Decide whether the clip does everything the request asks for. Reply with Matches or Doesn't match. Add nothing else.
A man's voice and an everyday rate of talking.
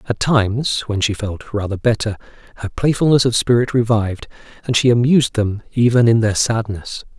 Matches